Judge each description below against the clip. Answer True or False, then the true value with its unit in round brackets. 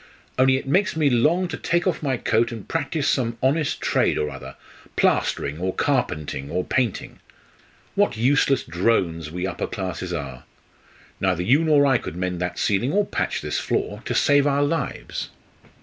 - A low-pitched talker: True (120 Hz)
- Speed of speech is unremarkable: True (170 wpm)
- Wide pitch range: True (8.3 semitones)